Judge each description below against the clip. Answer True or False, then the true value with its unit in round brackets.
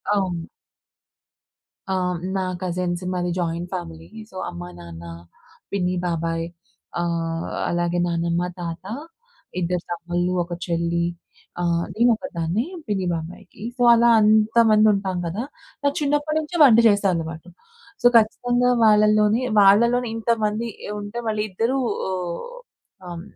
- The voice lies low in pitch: False (185 Hz)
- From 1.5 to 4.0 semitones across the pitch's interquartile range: False (4.4 semitones)